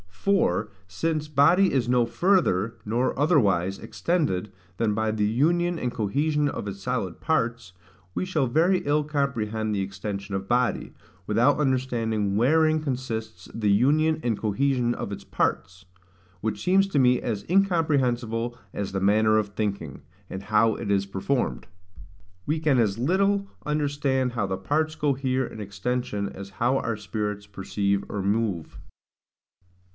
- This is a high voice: No, low, 120 Hz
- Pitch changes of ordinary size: No, wide, 6.2 semitones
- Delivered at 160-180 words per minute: No, average, 145 wpm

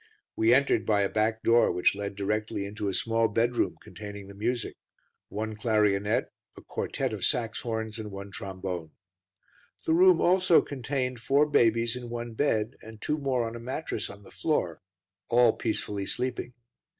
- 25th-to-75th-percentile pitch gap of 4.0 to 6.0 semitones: No, average, 3.1 semitones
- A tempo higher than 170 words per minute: No, average, 160 wpm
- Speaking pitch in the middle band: No, low, 110 Hz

